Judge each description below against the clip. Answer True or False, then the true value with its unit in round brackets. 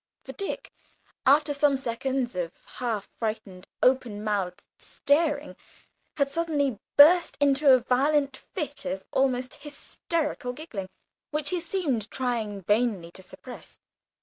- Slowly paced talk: True (120 wpm)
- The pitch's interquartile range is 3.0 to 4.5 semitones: False (5.1 semitones)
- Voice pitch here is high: True (265 Hz)